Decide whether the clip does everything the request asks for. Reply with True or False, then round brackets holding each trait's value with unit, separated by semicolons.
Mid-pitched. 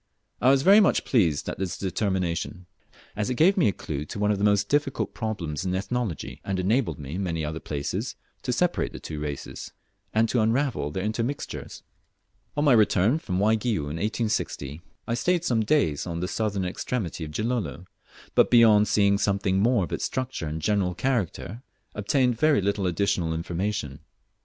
False (100 Hz)